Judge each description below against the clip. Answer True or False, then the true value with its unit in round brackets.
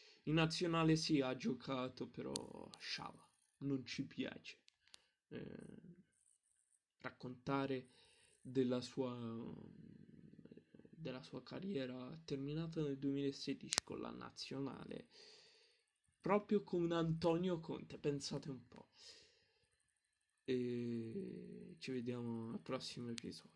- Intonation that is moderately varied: False (7.8 semitones)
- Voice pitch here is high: False (140 Hz)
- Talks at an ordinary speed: False (95 wpm)